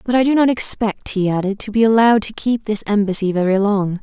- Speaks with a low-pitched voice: No, high, 210 Hz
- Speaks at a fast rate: Yes, fast, 240 wpm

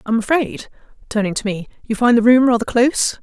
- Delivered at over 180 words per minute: Yes, fast, 205 wpm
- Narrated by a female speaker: Yes, female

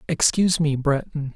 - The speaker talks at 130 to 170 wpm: Yes, slow, 135 wpm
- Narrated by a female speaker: No, male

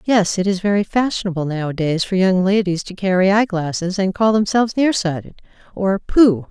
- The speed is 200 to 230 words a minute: Yes, fast, 205 wpm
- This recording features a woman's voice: Yes, female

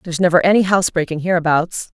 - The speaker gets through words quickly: No, average, 150 wpm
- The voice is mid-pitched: Yes, medium, 175 Hz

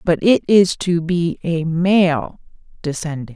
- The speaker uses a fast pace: No, average, 145 wpm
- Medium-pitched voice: Yes, medium, 170 Hz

